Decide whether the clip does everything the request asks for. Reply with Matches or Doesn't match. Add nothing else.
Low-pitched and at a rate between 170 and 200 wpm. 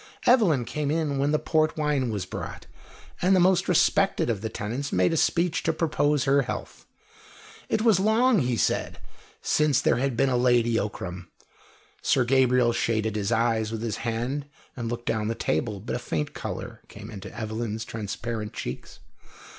Matches